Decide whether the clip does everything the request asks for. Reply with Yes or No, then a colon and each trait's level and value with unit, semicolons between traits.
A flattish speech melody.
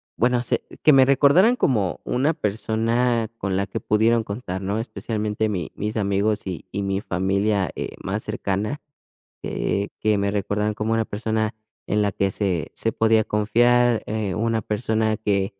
Yes: narrow, 2.3 semitones